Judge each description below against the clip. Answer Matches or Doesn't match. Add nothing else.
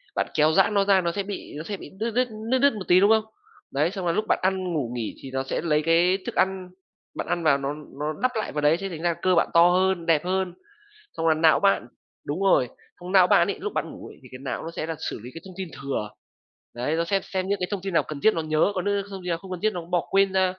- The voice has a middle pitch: Matches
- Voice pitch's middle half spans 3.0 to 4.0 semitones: Matches